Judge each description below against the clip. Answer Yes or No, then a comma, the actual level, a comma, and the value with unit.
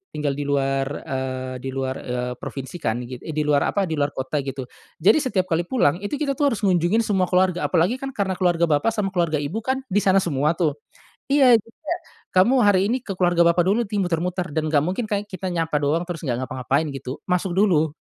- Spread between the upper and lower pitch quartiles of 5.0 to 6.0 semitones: Yes, wide, 5.6 semitones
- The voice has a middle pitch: Yes, medium, 175 Hz